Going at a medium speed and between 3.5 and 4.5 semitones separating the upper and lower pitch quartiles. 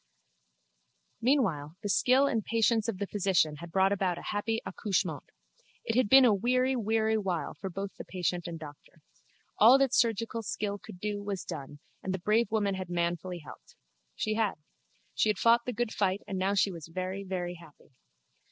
Yes: average, 180 wpm; average, 3.8 semitones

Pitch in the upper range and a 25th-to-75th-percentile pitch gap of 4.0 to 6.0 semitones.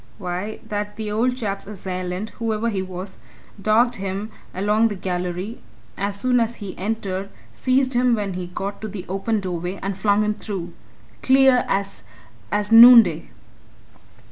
No: high, 205 Hz; average, 3.1 semitones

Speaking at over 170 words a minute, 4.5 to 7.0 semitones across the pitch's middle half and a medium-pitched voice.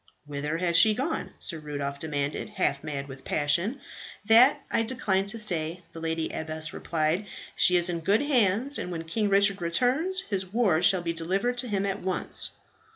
Yes: average, 180 wpm; wide, 5.4 semitones; medium, 180 Hz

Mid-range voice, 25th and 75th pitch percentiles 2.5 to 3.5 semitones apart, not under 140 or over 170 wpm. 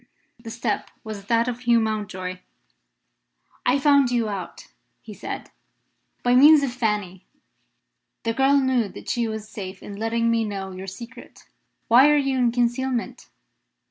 No: high, 230 Hz; average, 3.2 semitones; average, 150 wpm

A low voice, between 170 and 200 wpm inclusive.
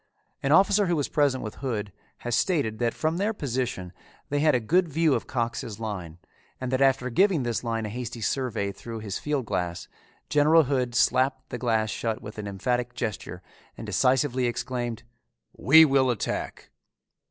Yes: low, 125 Hz; average, 175 wpm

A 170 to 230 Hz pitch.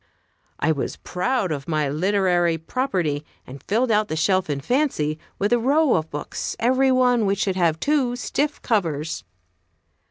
Yes: high, 190 Hz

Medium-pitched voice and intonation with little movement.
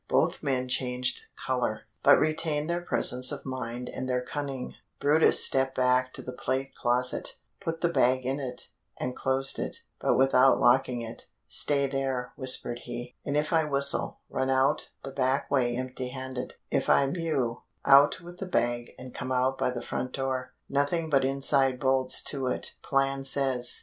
No: low, 130 Hz; narrow, 1.7 semitones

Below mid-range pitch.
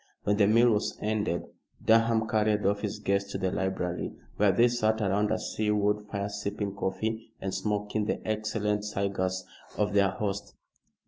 Yes: low, 105 Hz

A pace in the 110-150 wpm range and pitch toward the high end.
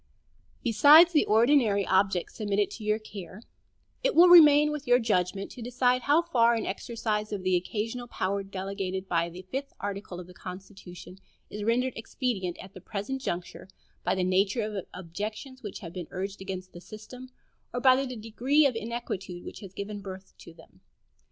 No: average, 175 wpm; high, 210 Hz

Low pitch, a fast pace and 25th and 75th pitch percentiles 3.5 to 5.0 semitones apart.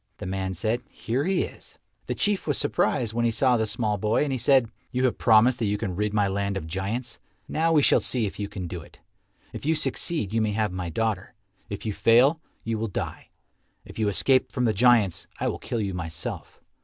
Yes: low, 110 Hz; fast, 230 wpm; average, 3.9 semitones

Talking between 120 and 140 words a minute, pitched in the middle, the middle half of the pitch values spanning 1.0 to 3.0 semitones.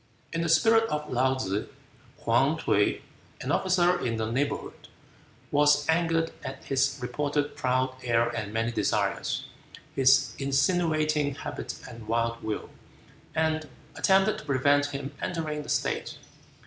No: slow, 135 wpm; medium, 145 Hz; average, 3.9 semitones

